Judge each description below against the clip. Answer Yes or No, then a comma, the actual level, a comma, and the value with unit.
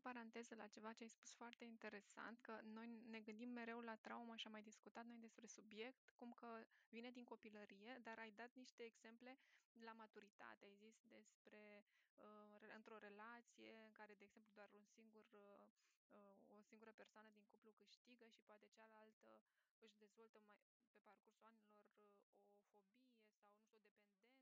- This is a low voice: No, high, 220 Hz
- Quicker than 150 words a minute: Yes, average, 165 wpm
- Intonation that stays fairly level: Yes, narrow, 1.8 semitones